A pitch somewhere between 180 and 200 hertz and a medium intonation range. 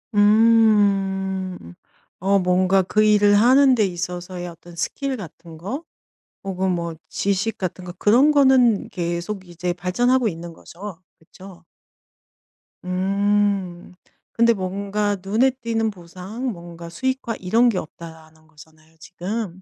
Yes: high, 190 Hz; average, 3.7 semitones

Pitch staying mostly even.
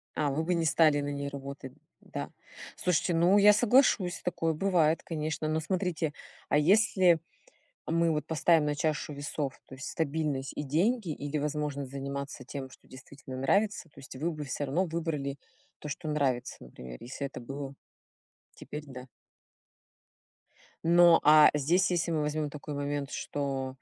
No: average, 3.1 semitones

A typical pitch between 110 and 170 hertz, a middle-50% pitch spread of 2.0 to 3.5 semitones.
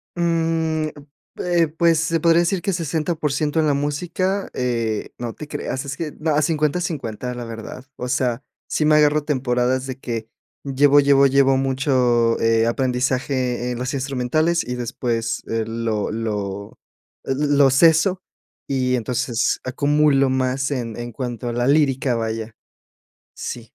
No: low, 135 Hz; average, 3.9 semitones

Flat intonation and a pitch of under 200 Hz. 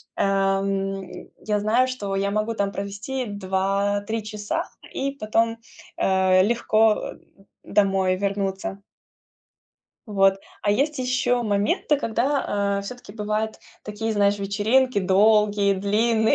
No: narrow, 2.3 semitones; high, 205 Hz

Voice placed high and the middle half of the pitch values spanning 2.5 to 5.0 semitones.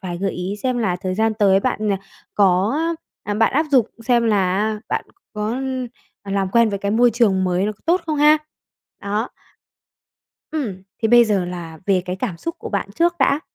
Yes: high, 210 Hz; average, 4.2 semitones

